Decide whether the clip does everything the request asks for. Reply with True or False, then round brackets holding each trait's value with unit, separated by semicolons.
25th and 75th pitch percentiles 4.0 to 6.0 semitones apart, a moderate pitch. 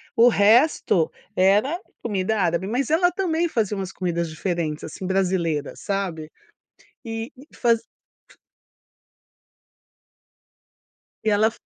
False (4.9 semitones; 200 Hz)